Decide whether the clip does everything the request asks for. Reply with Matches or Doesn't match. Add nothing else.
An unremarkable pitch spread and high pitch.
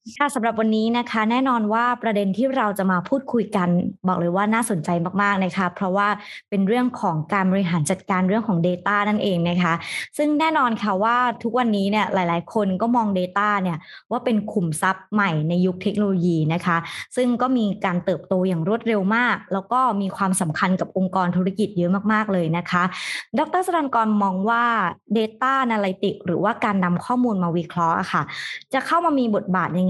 Matches